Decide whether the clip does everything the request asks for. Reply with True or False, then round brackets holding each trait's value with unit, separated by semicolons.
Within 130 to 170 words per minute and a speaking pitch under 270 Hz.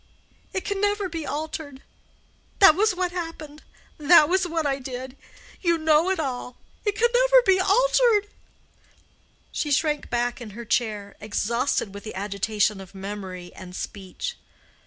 False (150 wpm; 300 Hz)